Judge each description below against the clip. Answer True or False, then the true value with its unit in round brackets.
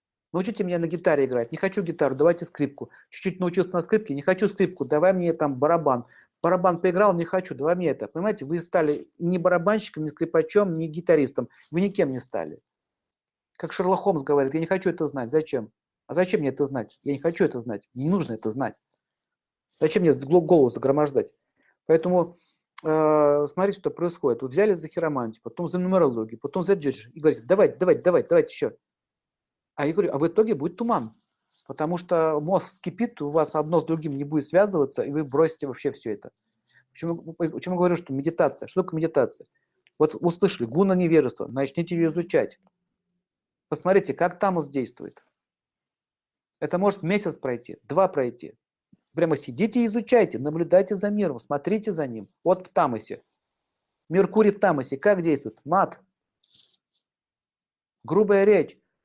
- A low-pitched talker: False (170 Hz)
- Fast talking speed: True (165 wpm)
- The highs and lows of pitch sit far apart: False (4.3 semitones)